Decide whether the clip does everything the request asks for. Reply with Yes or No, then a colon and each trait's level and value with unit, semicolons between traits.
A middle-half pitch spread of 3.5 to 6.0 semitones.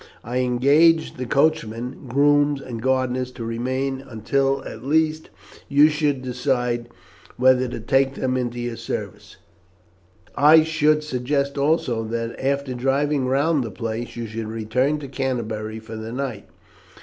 No: average, 3.0 semitones